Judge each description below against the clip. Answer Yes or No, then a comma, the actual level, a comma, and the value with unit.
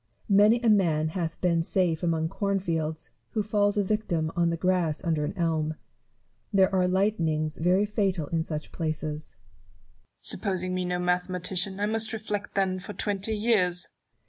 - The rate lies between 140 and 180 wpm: Yes, average, 165 wpm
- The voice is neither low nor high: Yes, medium, 180 Hz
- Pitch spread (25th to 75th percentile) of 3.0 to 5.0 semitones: Yes, average, 3.6 semitones